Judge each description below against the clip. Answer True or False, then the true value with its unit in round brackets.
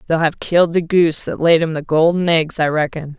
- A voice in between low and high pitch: True (160 Hz)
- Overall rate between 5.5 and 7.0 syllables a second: True (5.7 syllables/s)